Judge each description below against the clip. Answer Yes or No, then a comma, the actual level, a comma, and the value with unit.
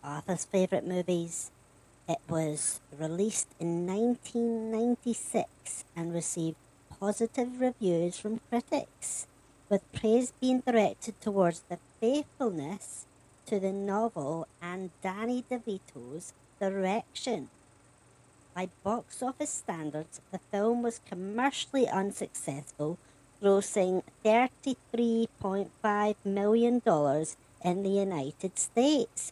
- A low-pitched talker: No, high, 195 Hz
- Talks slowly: Yes, slow, 90 wpm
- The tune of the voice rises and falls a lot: Yes, wide, 6.2 semitones